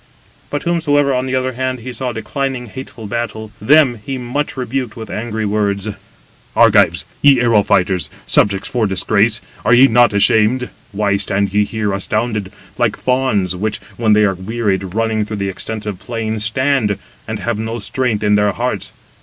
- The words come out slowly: No, average, 170 wpm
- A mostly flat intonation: No, average, 3.5 semitones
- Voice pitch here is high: No, low, 110 Hz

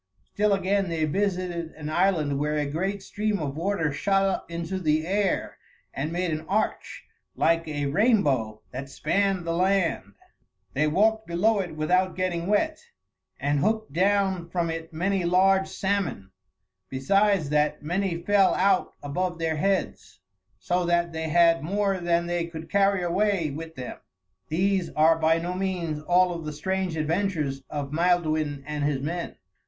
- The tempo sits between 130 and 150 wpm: No, average, 160 wpm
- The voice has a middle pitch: Yes, medium, 170 Hz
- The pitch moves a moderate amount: Yes, average, 3.8 semitones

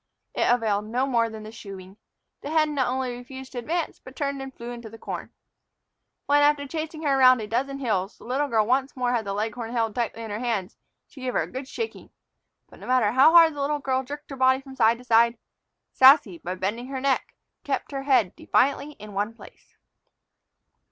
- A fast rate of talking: Yes, fast, 215 wpm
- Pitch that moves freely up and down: No, average, 3.5 semitones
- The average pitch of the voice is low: No, very high, 255 Hz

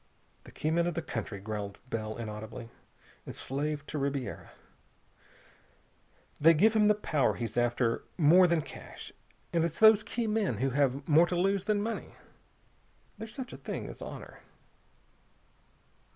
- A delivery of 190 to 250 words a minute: No, average, 150 wpm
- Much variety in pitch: Yes, wide, 8.3 semitones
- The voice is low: No, medium, 150 Hz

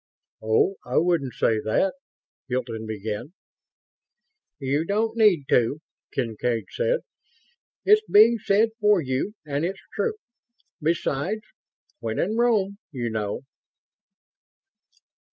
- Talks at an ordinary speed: No, slow, 110 wpm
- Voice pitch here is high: No, medium, 155 Hz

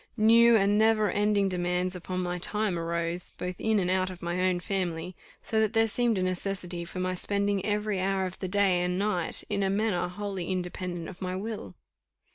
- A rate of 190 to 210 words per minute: Yes, average, 200 wpm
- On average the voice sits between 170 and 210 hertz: Yes, medium, 185 Hz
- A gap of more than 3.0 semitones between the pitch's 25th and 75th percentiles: No, narrow, 2.4 semitones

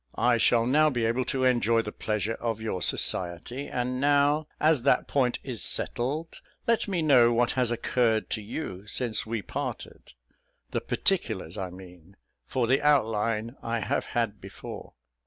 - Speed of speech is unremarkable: Yes, average, 160 wpm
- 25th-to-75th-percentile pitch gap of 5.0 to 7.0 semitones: No, average, 3.6 semitones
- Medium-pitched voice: No, low, 120 Hz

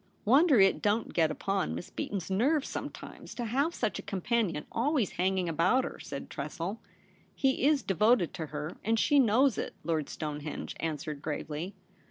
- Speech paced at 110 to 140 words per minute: No, average, 175 wpm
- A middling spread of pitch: No, wide, 7.3 semitones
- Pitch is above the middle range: Yes, high, 195 Hz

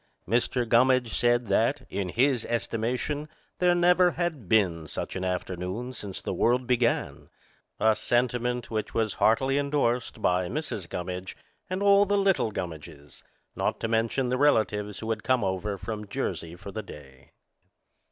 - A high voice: No, low, 115 Hz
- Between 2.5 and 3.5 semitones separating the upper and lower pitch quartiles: No, average, 4.8 semitones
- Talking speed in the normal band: Yes, average, 150 wpm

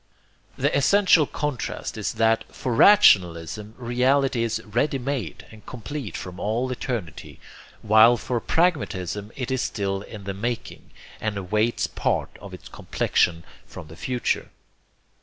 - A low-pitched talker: Yes, low, 115 Hz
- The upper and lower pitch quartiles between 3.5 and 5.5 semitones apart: Yes, average, 4.2 semitones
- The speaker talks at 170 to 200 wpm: No, slow, 135 wpm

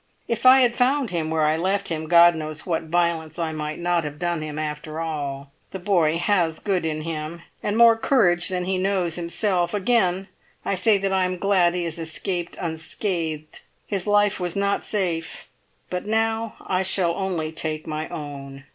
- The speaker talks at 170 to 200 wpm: Yes, average, 185 wpm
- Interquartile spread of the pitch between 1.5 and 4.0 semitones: Yes, average, 3.7 semitones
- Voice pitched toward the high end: No, medium, 175 Hz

